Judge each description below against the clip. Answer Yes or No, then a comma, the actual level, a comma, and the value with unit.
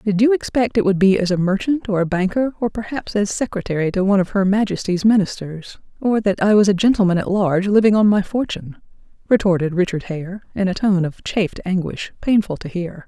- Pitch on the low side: No, high, 195 Hz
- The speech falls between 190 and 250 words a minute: Yes, fast, 205 wpm